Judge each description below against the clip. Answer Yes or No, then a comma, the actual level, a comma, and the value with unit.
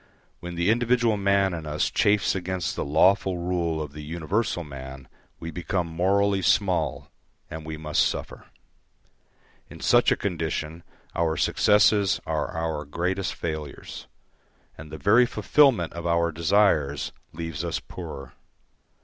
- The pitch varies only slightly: No, average, 3.9 semitones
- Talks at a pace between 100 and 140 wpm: Yes, slow, 135 wpm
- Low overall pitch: Yes, very low, 85 Hz